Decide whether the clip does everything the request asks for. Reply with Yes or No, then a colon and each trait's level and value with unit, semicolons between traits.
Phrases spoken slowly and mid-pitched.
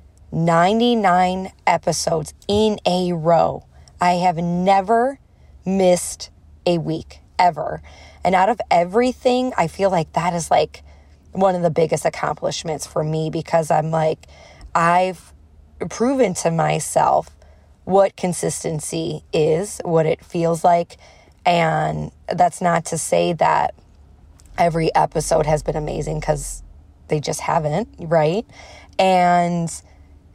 Yes: slow, 120 wpm; medium, 165 Hz